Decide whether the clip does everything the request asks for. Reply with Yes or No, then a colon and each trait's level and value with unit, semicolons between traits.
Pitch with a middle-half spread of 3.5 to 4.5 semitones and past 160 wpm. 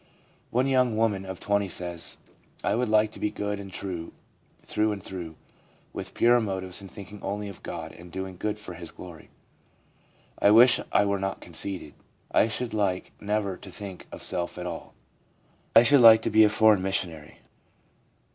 No: average, 3.0 semitones; average, 185 wpm